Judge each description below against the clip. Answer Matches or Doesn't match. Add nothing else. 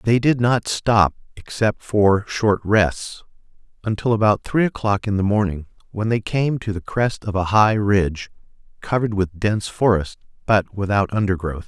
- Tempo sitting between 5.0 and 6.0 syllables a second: Doesn't match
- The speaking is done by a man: Matches